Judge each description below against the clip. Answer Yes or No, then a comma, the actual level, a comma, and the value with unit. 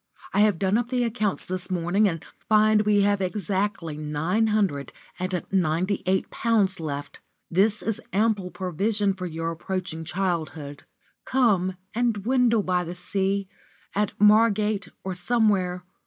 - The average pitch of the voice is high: Yes, high, 195 Hz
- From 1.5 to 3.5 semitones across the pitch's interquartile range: Yes, average, 3.0 semitones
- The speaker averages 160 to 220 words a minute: No, average, 140 wpm